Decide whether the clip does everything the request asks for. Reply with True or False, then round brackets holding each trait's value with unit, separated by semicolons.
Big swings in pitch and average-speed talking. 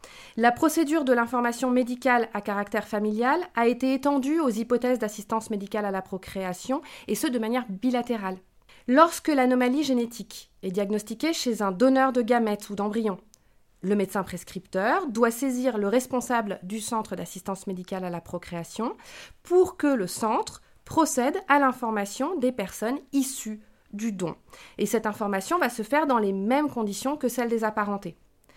False (4.3 semitones; 160 wpm)